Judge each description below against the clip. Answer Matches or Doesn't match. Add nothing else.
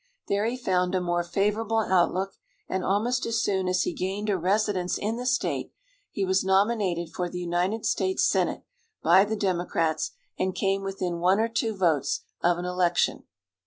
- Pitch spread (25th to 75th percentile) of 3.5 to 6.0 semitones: Doesn't match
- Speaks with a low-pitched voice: Doesn't match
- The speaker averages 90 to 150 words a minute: Doesn't match